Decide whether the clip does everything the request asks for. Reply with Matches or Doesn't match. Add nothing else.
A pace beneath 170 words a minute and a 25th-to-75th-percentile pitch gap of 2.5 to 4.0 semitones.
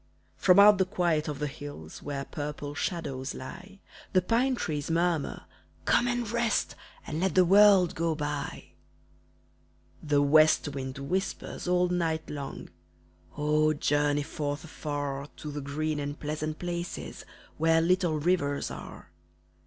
Matches